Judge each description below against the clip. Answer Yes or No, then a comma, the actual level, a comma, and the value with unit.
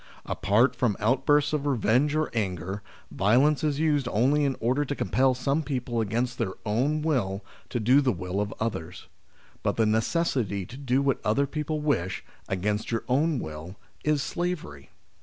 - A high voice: No, low, 125 Hz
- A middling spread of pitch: No, wide, 5.7 semitones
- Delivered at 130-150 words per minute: No, average, 165 wpm